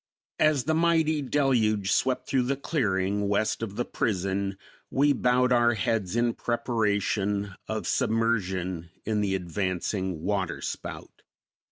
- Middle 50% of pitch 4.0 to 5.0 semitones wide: Yes, average, 4.4 semitones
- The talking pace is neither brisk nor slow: No, slow, 125 wpm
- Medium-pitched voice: No, low, 110 Hz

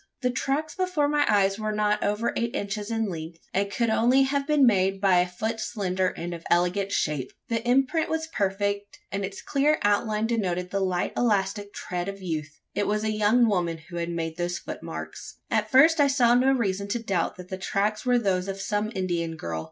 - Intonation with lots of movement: No, average, 4.2 semitones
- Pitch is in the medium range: No, high, 205 Hz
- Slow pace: No, fast, 205 wpm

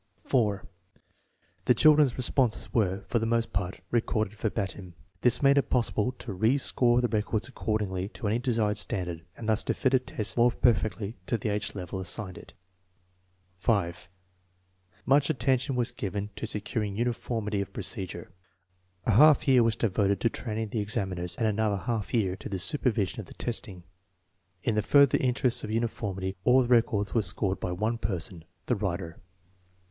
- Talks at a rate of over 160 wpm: Yes, average, 175 wpm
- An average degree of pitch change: Yes, average, 3.5 semitones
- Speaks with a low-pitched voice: Yes, low, 110 Hz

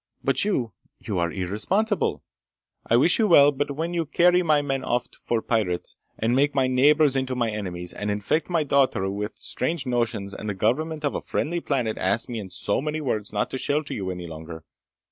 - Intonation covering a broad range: Yes, wide, 6.5 semitones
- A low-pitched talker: Yes, low, 125 Hz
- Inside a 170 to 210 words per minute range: Yes, average, 200 wpm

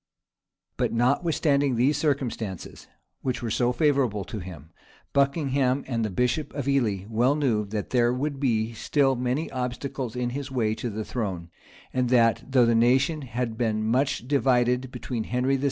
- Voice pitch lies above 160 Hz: No, low, 125 Hz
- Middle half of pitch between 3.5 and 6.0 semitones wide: No, average, 3.1 semitones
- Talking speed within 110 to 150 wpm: No, average, 165 wpm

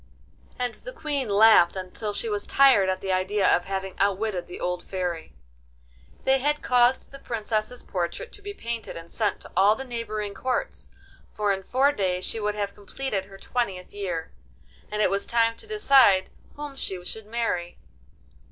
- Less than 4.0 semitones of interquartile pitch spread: No, average, 4.7 semitones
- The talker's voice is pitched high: Yes, high, 210 Hz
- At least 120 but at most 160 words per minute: No, average, 175 wpm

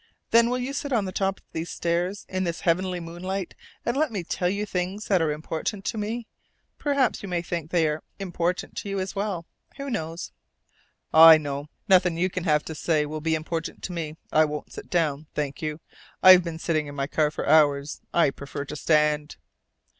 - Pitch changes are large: No, average, 3.7 semitones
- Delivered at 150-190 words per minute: No, fast, 205 wpm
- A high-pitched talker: No, medium, 170 Hz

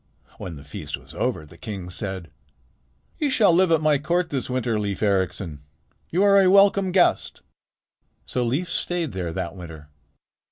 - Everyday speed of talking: Yes, average, 165 wpm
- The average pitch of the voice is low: Yes, low, 125 Hz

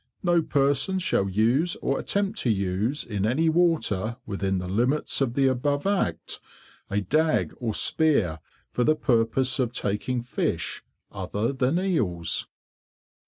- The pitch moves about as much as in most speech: No, wide, 7.0 semitones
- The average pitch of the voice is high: No, low, 125 Hz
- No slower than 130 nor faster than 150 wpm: Yes, average, 140 wpm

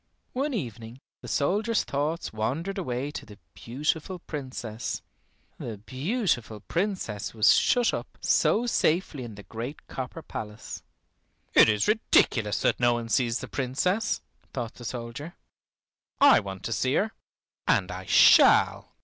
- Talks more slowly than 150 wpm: Yes, average, 140 wpm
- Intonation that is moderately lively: No, wide, 7.4 semitones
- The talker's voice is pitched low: Yes, low, 130 Hz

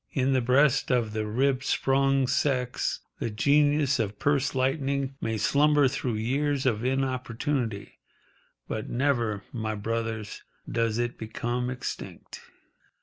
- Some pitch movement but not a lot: Yes, average, 3.4 semitones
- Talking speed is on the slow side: Yes, slow, 125 wpm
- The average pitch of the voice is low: Yes, low, 130 Hz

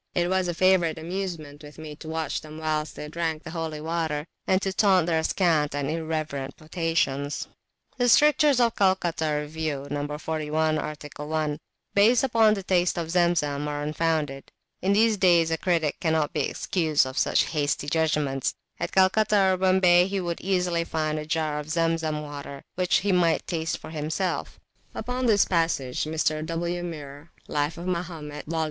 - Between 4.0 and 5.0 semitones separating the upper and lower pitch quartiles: No, average, 3.0 semitones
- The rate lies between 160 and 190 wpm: Yes, average, 175 wpm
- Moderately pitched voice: Yes, medium, 160 Hz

